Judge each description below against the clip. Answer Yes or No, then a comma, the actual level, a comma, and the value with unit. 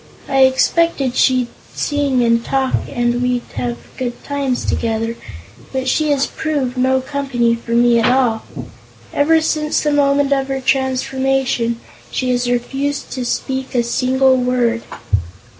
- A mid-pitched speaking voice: No, very high, 260 Hz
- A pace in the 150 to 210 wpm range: No, average, 140 wpm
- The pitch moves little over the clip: Yes, narrow, 2.1 semitones